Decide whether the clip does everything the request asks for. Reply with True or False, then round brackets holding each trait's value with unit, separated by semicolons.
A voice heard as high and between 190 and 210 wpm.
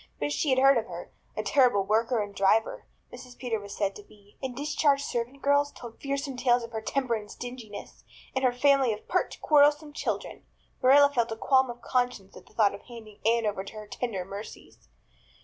True (240 Hz; 205 wpm)